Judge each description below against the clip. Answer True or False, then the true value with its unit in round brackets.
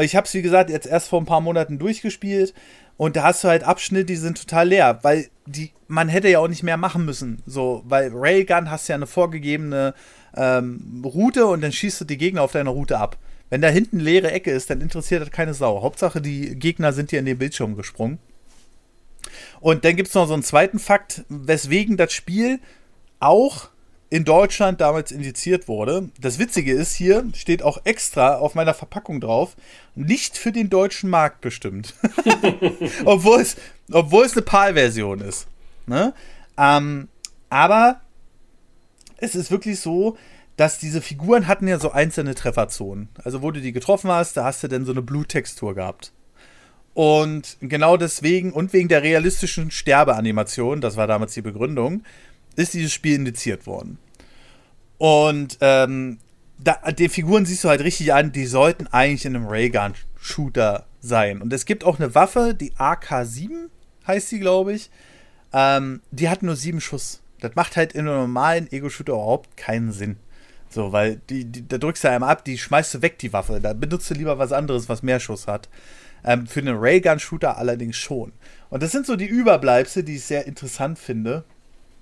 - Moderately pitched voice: True (150 Hz)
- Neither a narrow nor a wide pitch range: False (5.8 semitones)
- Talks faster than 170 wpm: True (180 wpm)